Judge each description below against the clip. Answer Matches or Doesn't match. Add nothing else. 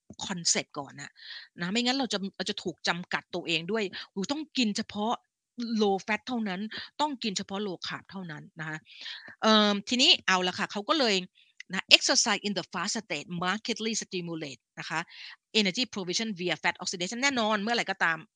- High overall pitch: Matches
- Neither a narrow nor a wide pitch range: Matches